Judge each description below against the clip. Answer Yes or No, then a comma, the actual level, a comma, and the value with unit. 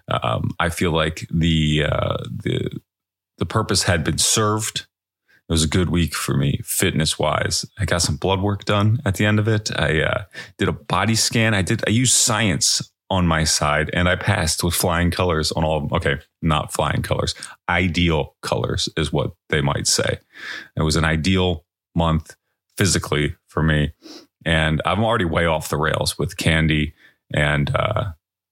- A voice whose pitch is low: Yes, very low, 85 Hz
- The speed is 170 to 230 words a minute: Yes, average, 180 wpm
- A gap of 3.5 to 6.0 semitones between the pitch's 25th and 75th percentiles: Yes, average, 4.5 semitones